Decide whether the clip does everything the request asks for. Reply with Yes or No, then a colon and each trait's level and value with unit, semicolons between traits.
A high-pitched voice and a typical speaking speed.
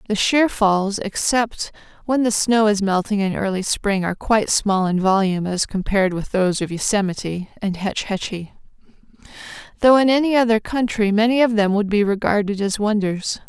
Yes: high, 205 Hz; average, 175 wpm